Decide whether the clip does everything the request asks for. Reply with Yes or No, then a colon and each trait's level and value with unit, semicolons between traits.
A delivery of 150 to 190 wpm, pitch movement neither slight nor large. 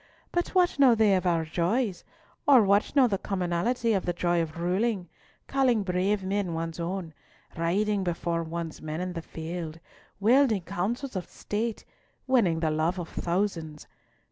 Yes: average, 160 wpm; average, 4.2 semitones